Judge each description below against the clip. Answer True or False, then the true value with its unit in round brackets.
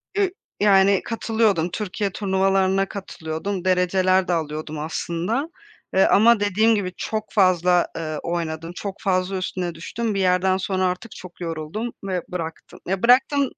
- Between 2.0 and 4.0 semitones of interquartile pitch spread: True (2.8 semitones)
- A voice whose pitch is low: False (190 Hz)